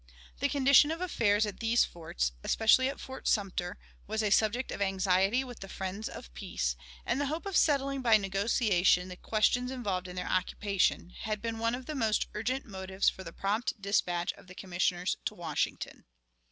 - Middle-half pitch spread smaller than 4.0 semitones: No, average, 4.8 semitones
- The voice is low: No, high, 210 Hz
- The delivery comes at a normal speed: Yes, average, 185 wpm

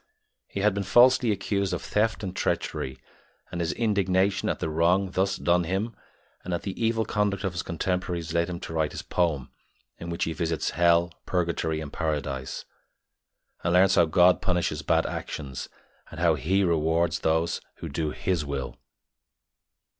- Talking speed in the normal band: Yes, average, 170 wpm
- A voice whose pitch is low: Yes, very low, 85 Hz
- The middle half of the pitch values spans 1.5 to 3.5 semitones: Yes, average, 3.0 semitones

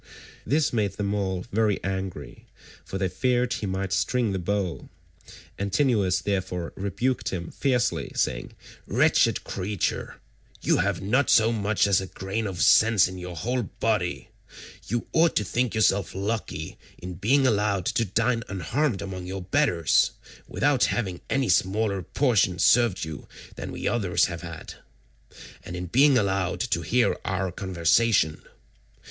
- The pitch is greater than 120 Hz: No, low, 100 Hz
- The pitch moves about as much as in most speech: Yes, average, 4.0 semitones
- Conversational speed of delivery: Yes, average, 145 wpm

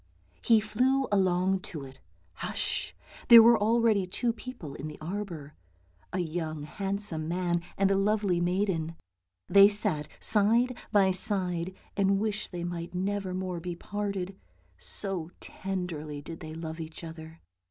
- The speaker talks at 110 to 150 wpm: Yes, average, 140 wpm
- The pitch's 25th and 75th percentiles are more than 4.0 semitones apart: No, average, 3.7 semitones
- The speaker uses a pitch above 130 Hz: Yes, medium, 185 Hz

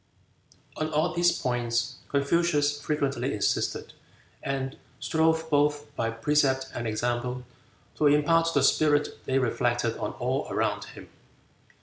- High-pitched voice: No, medium, 145 Hz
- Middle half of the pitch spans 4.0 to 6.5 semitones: No, average, 3.6 semitones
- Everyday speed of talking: No, slow, 120 wpm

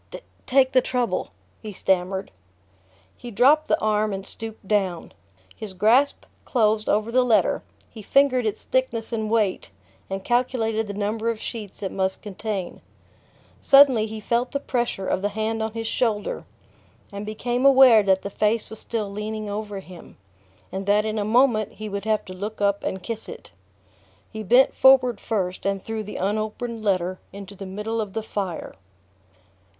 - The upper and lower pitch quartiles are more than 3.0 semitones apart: No, narrow, 2.5 semitones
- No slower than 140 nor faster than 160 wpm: No, average, 170 wpm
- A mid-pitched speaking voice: No, high, 215 Hz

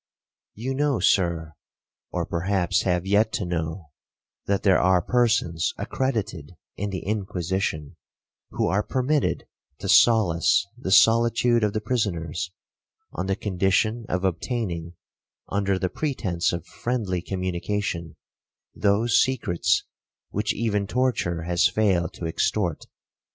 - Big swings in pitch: No, average, 4.2 semitones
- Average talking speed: No, slow, 120 wpm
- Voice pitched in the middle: No, low, 100 Hz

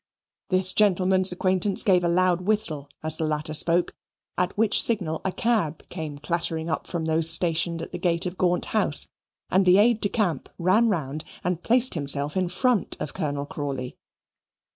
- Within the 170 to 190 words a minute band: Yes, average, 175 wpm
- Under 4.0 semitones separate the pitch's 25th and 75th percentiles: Yes, average, 3.1 semitones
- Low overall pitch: No, medium, 175 Hz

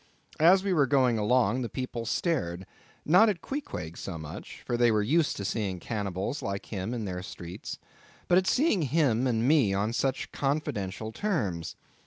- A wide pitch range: Yes, wide, 7.3 semitones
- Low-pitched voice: Yes, low, 120 Hz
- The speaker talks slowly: No, average, 165 wpm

